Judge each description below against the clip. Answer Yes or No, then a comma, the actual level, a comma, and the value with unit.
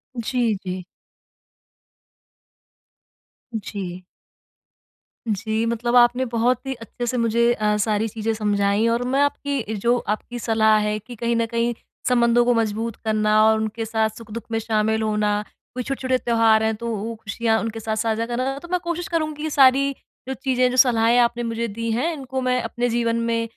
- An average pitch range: No, narrow, 2.2 semitones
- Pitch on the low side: No, high, 230 Hz